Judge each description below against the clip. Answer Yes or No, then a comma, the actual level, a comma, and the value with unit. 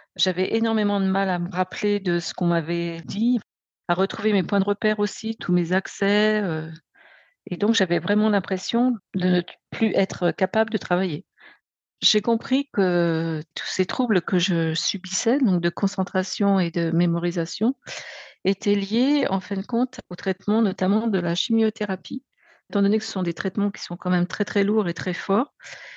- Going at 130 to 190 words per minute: Yes, average, 185 wpm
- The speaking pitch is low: No, high, 195 Hz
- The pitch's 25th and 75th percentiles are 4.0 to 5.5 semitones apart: No, average, 3.3 semitones